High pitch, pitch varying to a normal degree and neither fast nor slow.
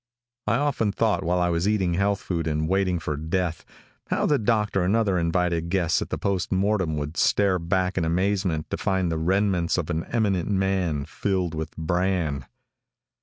No: very low, 90 Hz; average, 3.0 semitones; average, 180 wpm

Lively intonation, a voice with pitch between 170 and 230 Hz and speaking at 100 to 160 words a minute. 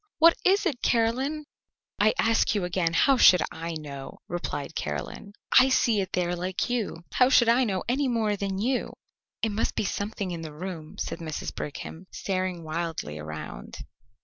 No: wide, 6.1 semitones; high, 190 Hz; average, 175 wpm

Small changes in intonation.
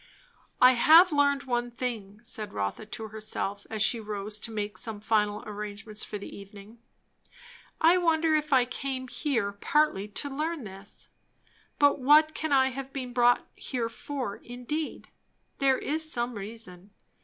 No: average, 5.2 semitones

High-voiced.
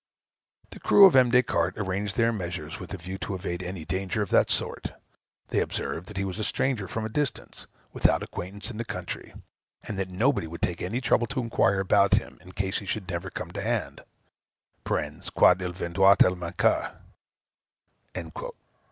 No: very low, 95 Hz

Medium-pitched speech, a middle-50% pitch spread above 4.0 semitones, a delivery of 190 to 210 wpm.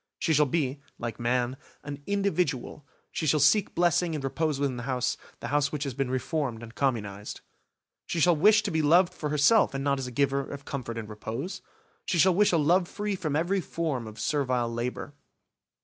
Yes: medium, 145 Hz; average, 5.0 semitones; average, 200 wpm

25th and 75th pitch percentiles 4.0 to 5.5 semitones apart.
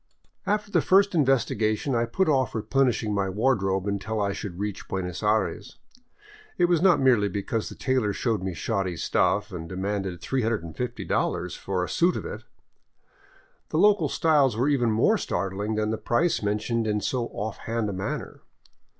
Yes: average, 4.9 semitones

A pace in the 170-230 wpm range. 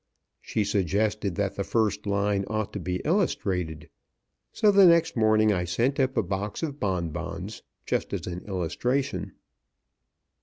No: average, 145 wpm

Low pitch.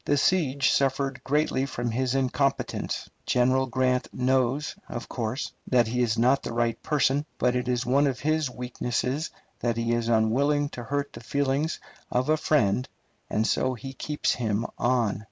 Yes: low, 130 Hz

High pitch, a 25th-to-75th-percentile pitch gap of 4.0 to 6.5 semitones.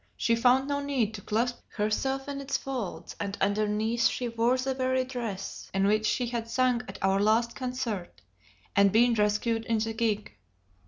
No: high, 230 Hz; average, 3.2 semitones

